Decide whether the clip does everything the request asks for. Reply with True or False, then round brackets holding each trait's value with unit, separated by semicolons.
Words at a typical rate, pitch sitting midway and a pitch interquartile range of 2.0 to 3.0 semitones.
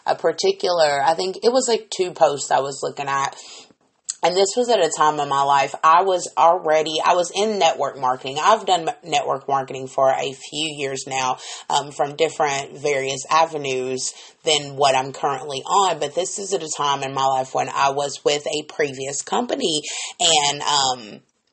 False (185 wpm; 145 Hz; 3.8 semitones)